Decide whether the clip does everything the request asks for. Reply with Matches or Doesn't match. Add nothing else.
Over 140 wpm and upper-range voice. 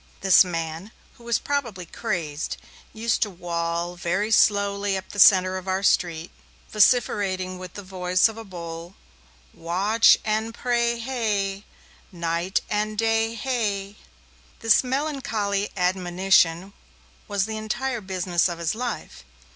Doesn't match